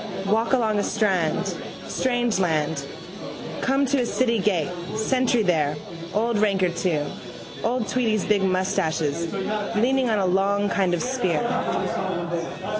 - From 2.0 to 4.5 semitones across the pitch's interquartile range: No, average, 5.0 semitones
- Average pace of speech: No, slow, 130 wpm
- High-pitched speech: Yes, high, 200 Hz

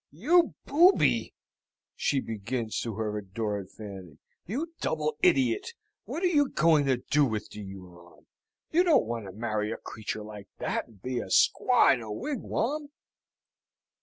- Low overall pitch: Yes, low, 120 Hz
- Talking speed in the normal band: Yes, average, 155 wpm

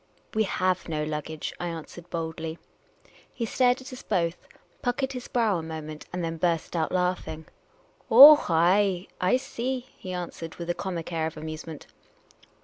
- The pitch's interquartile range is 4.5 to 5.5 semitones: Yes, average, 5.2 semitones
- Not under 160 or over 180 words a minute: Yes, average, 170 wpm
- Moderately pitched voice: Yes, medium, 175 Hz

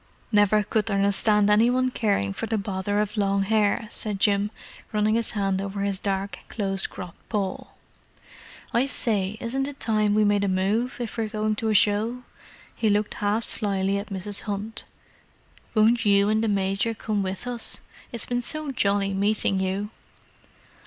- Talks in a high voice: Yes, high, 210 Hz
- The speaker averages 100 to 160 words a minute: No, average, 170 wpm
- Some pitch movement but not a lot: No, narrow, 1.9 semitones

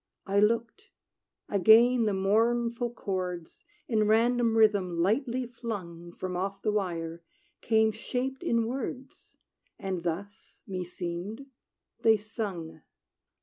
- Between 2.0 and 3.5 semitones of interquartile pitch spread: No, average, 4.2 semitones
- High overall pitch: Yes, high, 210 Hz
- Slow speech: Yes, slow, 105 wpm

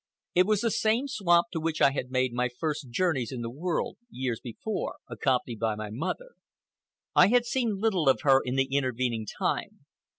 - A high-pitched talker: No, medium, 140 Hz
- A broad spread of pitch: Yes, wide, 7.7 semitones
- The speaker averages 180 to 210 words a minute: Yes, average, 190 wpm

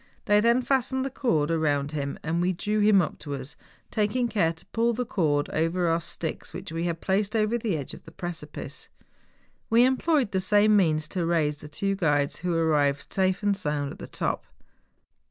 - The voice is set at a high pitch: No, medium, 175 Hz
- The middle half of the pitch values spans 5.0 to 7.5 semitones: Yes, wide, 5.6 semitones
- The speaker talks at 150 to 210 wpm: Yes, fast, 205 wpm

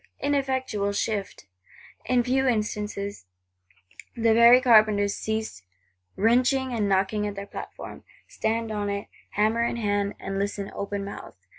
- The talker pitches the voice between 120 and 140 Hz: No, high, 210 Hz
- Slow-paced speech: Yes, slow, 130 wpm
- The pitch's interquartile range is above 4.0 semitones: No, narrow, 2.6 semitones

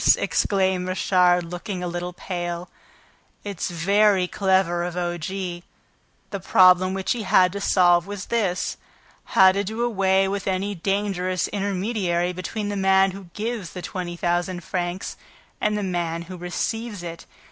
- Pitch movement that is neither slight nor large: No, narrow, 2.0 semitones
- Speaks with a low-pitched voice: No, medium, 185 Hz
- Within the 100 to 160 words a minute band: Yes, average, 150 wpm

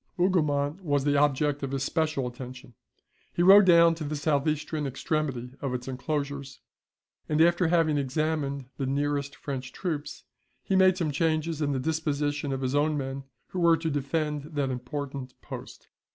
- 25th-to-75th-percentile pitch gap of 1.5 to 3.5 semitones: Yes, narrow, 2.6 semitones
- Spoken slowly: No, average, 165 wpm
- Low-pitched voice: No, medium, 145 Hz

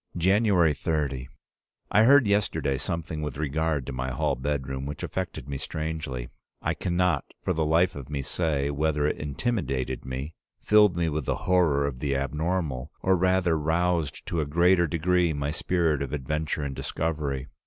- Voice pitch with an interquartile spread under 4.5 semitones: Yes, average, 3.9 semitones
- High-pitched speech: No, very low, 75 Hz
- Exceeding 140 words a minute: Yes, average, 170 wpm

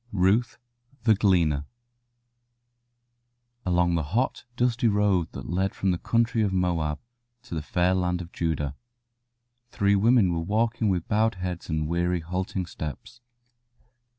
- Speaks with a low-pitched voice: Yes, very low, 90 Hz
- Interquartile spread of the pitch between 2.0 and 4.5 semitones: Yes, average, 3.9 semitones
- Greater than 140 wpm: No, slow, 135 wpm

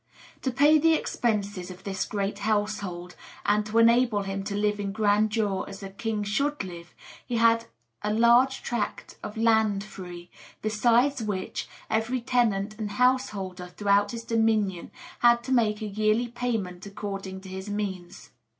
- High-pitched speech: Yes, high, 210 Hz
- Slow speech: No, average, 155 wpm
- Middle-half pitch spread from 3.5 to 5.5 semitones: No, average, 2.8 semitones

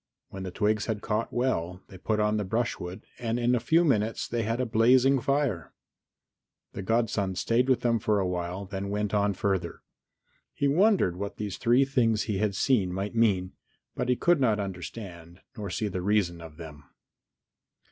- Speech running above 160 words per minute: Yes, average, 180 wpm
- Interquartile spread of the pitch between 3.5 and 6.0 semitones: Yes, average, 4.0 semitones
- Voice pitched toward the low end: Yes, low, 105 Hz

